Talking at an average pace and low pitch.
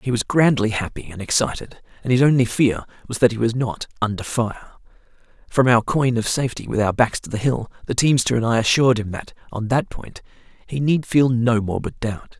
No: fast, 215 wpm; low, 120 Hz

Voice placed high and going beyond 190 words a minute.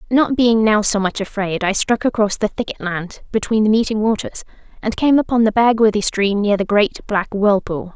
Yes: high, 215 Hz; fast, 205 wpm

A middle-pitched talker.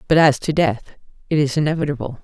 Yes: medium, 145 Hz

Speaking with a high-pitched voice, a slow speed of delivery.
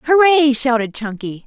Yes: very high, 265 Hz; slow, 125 wpm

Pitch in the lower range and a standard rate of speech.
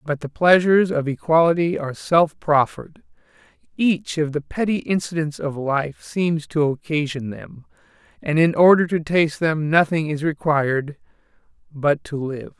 No: medium, 155 Hz; average, 150 wpm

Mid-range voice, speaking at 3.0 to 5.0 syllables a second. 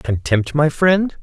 Yes: medium, 145 Hz; 3.5 syllables/s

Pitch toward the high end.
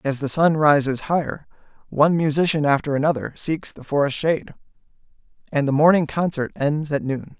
No: medium, 150 Hz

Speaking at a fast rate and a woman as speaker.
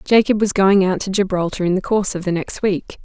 Yes: fast, 255 wpm; female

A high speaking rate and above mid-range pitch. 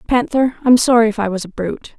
Yes: fast, 240 wpm; high, 225 Hz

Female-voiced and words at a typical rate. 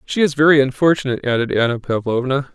No: male; average, 165 wpm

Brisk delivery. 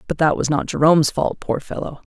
Yes: fast, 230 wpm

